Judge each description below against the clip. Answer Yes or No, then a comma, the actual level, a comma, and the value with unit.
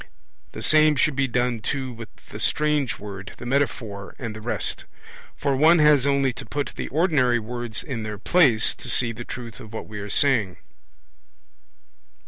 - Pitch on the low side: Yes, low, 125 Hz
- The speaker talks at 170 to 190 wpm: Yes, average, 175 wpm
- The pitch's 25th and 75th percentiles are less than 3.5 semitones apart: No, average, 4.3 semitones